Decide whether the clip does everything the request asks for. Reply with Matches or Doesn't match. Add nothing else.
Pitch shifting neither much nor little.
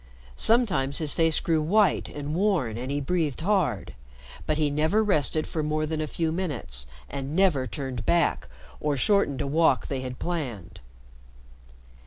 Matches